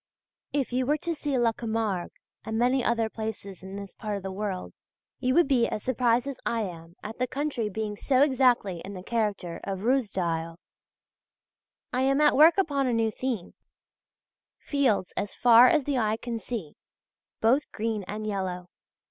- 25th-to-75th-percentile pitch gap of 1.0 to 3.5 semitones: No, average, 4.5 semitones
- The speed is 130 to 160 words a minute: No, average, 175 wpm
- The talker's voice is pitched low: No, high, 225 Hz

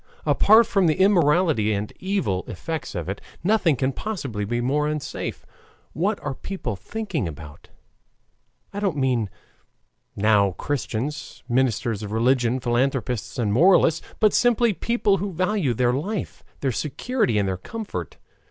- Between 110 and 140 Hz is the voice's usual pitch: Yes, low, 135 Hz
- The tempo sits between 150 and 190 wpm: No, average, 140 wpm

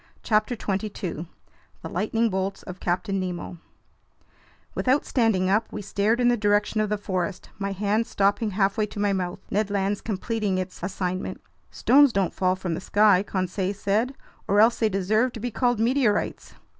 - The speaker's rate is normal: Yes, average, 170 wpm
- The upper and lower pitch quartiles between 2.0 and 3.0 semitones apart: Yes, average, 2.7 semitones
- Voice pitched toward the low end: No, high, 205 Hz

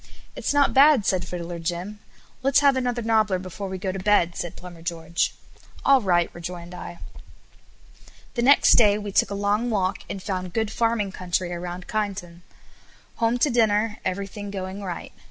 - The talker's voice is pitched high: Yes, high, 200 Hz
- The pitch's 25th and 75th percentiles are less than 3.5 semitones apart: No, average, 3.8 semitones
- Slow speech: No, average, 170 wpm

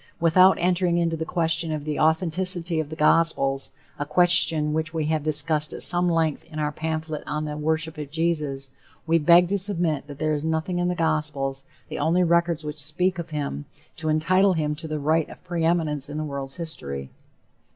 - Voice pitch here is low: No, medium, 160 Hz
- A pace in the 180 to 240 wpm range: Yes, average, 195 wpm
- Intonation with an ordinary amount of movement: No, narrow, 2.1 semitones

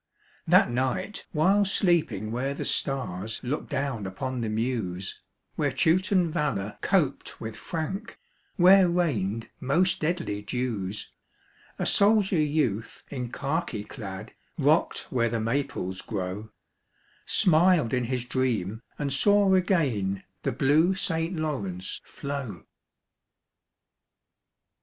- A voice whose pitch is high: No, low, 135 Hz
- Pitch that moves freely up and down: Yes, wide, 7.3 semitones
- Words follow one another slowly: Yes, slow, 110 wpm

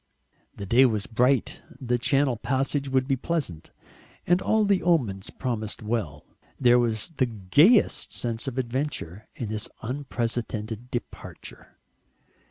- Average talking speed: No, slow, 130 wpm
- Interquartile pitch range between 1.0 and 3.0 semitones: No, average, 3.8 semitones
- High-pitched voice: No, low, 120 Hz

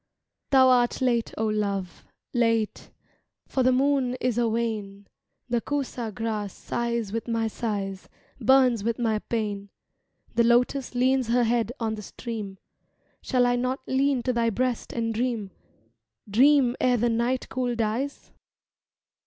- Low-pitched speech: No, high, 235 Hz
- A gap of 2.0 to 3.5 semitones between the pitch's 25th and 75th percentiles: Yes, narrow, 2.5 semitones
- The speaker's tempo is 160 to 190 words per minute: No, average, 145 wpm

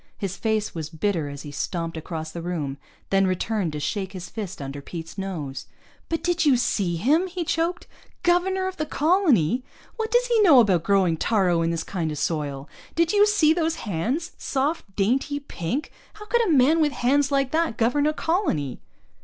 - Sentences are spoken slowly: No, average, 190 wpm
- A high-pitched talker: Yes, high, 220 Hz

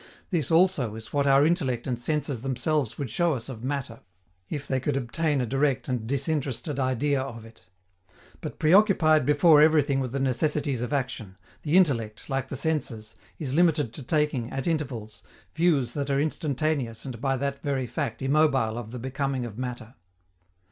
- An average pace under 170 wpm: No, average, 175 wpm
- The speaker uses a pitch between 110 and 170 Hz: Yes, low, 135 Hz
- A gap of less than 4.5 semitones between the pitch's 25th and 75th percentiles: Yes, average, 3.5 semitones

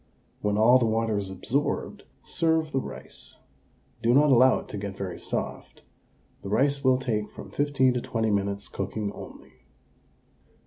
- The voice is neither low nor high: No, low, 115 Hz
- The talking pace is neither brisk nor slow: Yes, average, 160 wpm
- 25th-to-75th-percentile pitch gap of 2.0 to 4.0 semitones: No, average, 4.5 semitones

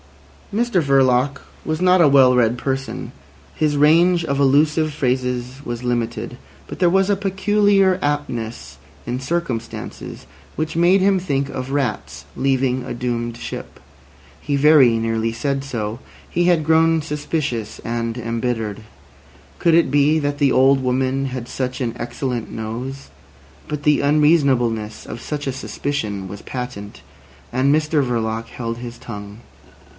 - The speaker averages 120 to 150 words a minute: Yes, average, 140 wpm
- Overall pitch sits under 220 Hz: Yes, low, 135 Hz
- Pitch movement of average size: Yes, average, 4.3 semitones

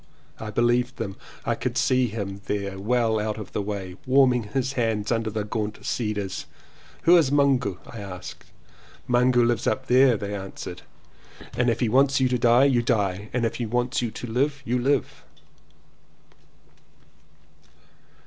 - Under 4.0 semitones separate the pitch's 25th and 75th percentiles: Yes, average, 3.2 semitones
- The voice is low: Yes, low, 120 Hz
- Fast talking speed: No, average, 165 wpm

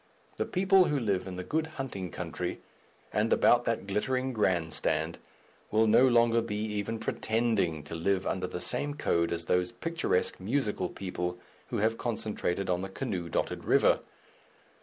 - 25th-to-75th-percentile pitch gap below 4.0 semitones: No, average, 4.7 semitones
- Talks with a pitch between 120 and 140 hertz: No, low, 105 Hz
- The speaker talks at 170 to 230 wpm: No, average, 160 wpm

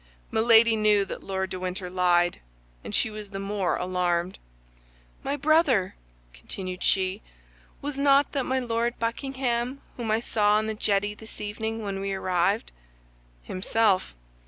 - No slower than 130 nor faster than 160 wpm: Yes, average, 145 wpm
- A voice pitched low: No, high, 210 Hz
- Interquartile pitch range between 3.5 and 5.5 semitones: Yes, average, 3.9 semitones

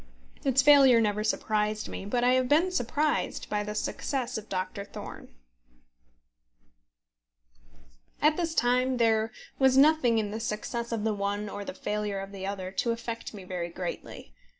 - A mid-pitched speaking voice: No, high, 225 Hz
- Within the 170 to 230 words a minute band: No, average, 160 wpm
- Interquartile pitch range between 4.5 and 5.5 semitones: No, average, 3.8 semitones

